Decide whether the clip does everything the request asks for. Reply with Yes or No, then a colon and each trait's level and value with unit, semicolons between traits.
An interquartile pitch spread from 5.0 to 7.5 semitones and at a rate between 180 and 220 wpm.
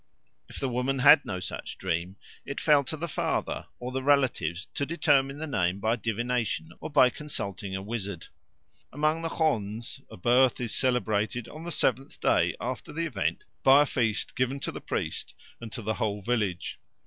Yes: wide, 5.5 semitones; average, 185 wpm